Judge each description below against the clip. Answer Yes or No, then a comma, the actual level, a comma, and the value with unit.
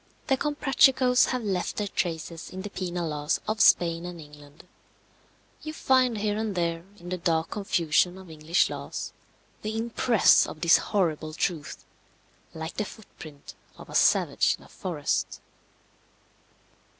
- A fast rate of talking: No, average, 150 wpm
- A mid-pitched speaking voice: Yes, medium, 180 Hz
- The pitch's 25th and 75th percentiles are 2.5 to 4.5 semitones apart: No, average, 5.0 semitones